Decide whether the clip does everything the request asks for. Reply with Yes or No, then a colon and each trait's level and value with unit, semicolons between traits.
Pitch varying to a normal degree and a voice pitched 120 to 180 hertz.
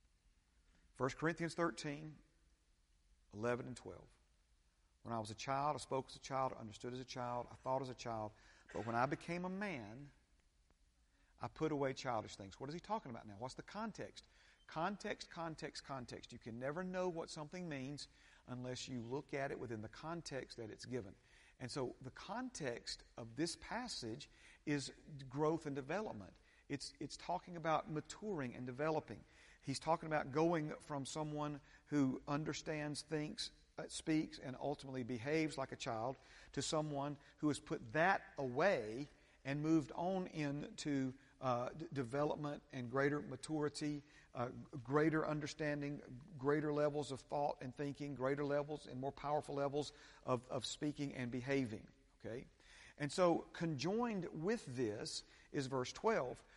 Yes: average, 3.5 semitones; medium, 140 Hz